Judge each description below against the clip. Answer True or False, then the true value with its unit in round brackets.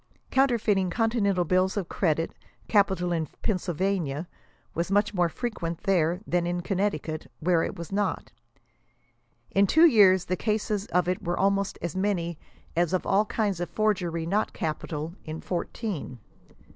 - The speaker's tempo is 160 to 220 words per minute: False (150 wpm)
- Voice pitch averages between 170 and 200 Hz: True (185 Hz)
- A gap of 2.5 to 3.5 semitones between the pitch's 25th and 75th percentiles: True (3.2 semitones)